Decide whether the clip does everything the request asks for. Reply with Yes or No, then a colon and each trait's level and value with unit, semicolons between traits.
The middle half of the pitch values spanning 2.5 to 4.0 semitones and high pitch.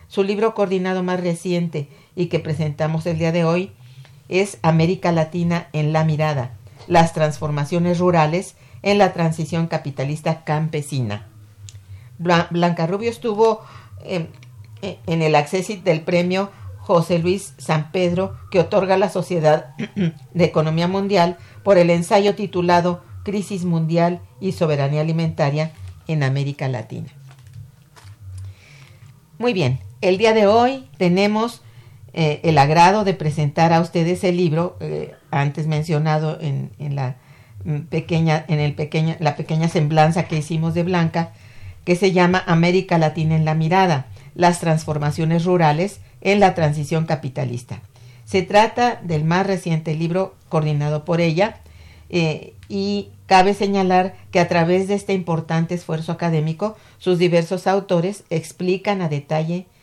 No: average, 3.5 semitones; medium, 165 Hz